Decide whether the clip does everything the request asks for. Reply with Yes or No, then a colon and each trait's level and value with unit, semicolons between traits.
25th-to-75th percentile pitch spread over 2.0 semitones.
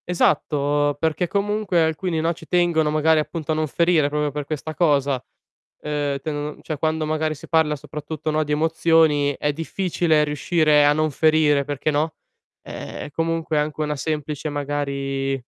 No: narrow, 1.6 semitones